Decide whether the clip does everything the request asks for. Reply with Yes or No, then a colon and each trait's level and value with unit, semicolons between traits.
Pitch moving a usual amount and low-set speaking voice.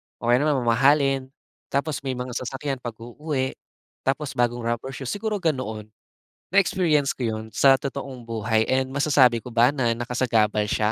Yes: average, 3.0 semitones; low, 130 Hz